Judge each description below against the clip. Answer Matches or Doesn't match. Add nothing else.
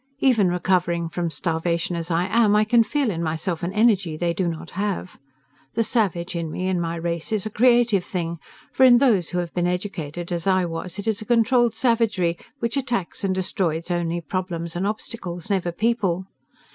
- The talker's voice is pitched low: Doesn't match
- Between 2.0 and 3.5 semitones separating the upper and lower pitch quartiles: Doesn't match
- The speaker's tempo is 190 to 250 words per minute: Matches